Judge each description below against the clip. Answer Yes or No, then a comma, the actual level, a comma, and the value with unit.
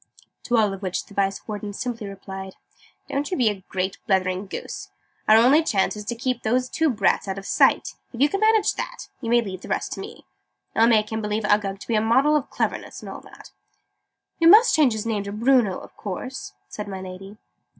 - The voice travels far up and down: No, average, 4.3 semitones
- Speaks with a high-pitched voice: Yes, high, 215 Hz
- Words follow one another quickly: Yes, fast, 225 wpm